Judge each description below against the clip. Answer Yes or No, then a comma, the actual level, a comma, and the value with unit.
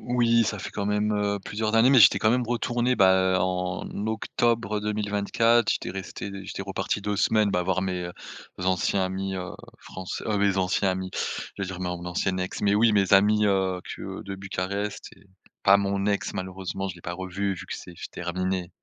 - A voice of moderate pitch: No, low, 100 Hz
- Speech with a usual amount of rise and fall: No, narrow, 2.1 semitones